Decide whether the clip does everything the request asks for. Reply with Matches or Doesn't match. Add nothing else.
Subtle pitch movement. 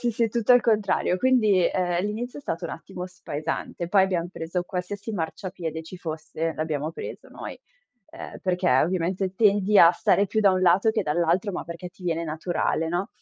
Doesn't match